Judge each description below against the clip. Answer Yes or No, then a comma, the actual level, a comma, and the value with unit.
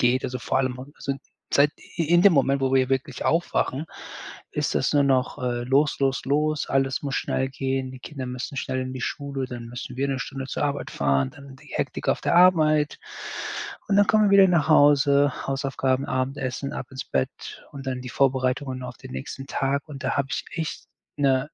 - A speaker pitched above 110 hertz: Yes, low, 135 Hz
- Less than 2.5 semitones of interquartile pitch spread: Yes, narrow, 1.8 semitones